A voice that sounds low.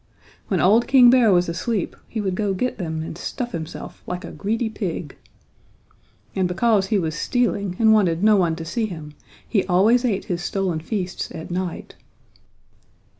No: high, 190 Hz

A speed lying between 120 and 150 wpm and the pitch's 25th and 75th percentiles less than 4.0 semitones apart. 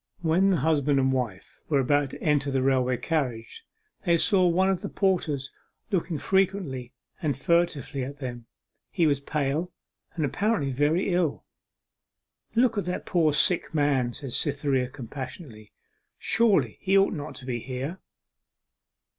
No: average, 145 wpm; average, 4.9 semitones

